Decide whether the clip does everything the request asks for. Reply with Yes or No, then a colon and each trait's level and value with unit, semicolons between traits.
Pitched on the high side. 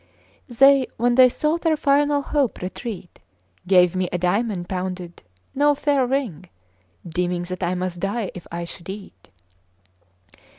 Yes: high, 195 Hz